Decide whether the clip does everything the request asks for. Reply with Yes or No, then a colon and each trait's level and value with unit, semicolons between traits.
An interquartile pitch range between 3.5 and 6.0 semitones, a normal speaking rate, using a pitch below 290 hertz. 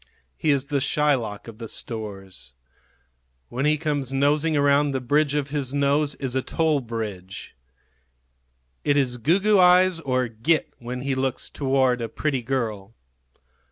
Yes: average, 3.8 semitones; average, 155 wpm; low, 135 Hz